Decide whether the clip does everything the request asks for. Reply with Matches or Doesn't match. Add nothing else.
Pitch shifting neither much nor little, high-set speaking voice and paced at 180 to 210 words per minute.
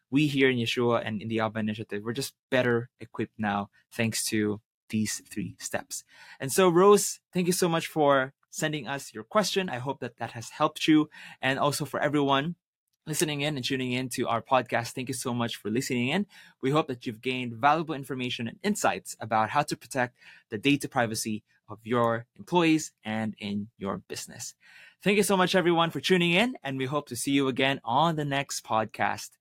Doesn't match